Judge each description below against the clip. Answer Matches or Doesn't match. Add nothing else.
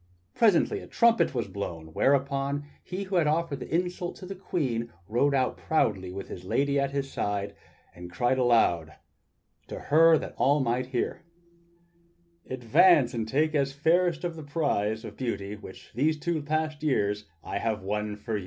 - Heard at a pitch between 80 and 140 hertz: Matches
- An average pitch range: Doesn't match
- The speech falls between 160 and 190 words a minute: Matches